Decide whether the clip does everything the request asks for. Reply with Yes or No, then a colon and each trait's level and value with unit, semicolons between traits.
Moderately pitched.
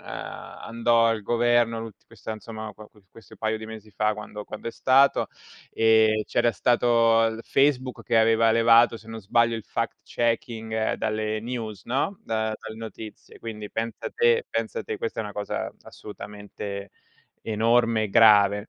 No: low, 115 Hz